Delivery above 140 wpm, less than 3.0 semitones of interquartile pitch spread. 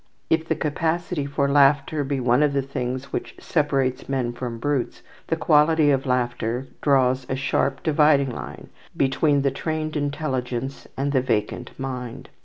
Yes: average, 155 wpm; narrow, 2.4 semitones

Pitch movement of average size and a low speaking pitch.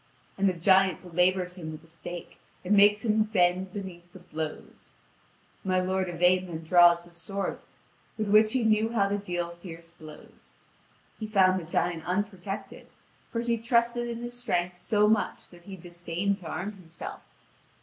No: average, 3.2 semitones; medium, 185 Hz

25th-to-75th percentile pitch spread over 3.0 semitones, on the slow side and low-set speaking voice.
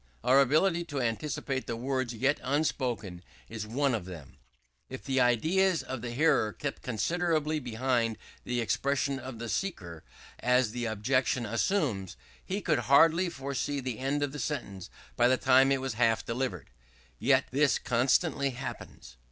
No: average, 3.6 semitones; average, 155 wpm; low, 130 Hz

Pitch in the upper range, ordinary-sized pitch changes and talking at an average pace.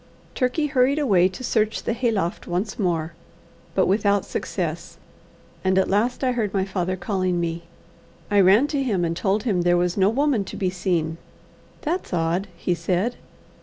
Yes: high, 195 Hz; average, 4.6 semitones; average, 170 wpm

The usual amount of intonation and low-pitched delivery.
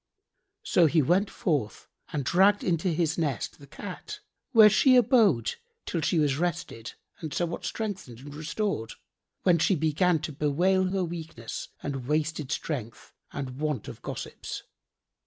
No: average, 4.5 semitones; medium, 160 Hz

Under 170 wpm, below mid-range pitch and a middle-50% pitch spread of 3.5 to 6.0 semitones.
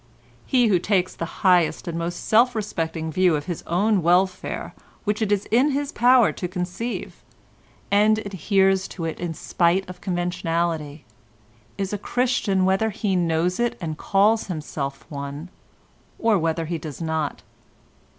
No: average, 150 wpm; medium, 185 Hz; average, 4.0 semitones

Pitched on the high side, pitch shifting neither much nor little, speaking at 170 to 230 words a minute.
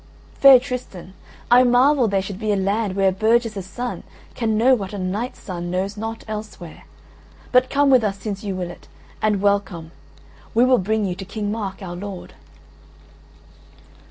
Yes: high, 205 Hz; average, 3.6 semitones; average, 175 wpm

